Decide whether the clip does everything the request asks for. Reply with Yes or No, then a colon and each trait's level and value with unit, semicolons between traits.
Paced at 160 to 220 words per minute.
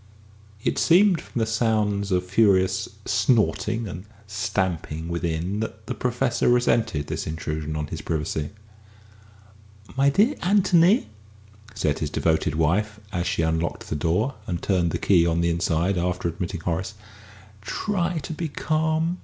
No: average, 145 wpm